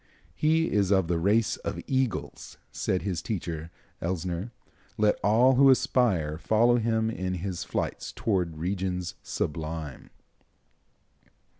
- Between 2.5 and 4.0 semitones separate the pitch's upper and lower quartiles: No, average, 5.1 semitones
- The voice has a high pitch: No, very low, 95 Hz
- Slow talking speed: Yes, slow, 120 wpm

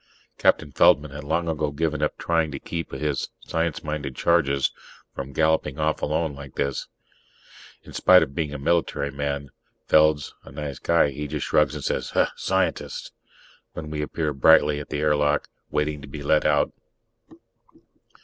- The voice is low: Yes, very low, 75 Hz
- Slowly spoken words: No, average, 160 wpm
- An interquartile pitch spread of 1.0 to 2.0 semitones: Yes, narrow, 1.6 semitones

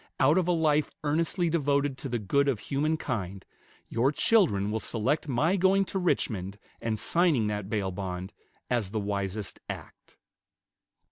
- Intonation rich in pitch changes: Yes, wide, 7.4 semitones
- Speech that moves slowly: No, average, 155 wpm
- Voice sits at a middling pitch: No, low, 130 Hz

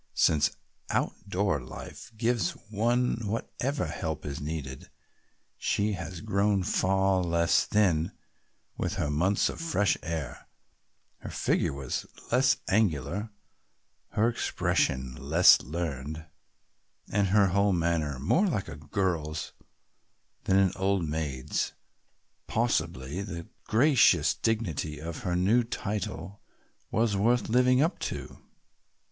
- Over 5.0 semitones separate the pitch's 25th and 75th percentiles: Yes, wide, 5.4 semitones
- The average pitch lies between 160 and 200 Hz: No, very low, 95 Hz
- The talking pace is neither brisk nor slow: No, slow, 115 wpm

